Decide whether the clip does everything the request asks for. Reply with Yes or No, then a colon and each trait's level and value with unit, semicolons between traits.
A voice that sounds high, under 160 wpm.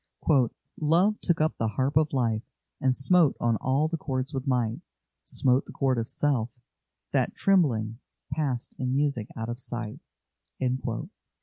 No: low, 130 Hz; average, 145 wpm